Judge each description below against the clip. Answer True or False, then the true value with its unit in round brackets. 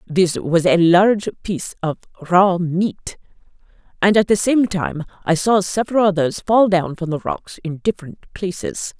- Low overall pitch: False (185 Hz)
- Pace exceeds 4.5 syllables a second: True (4.7 syllables/s)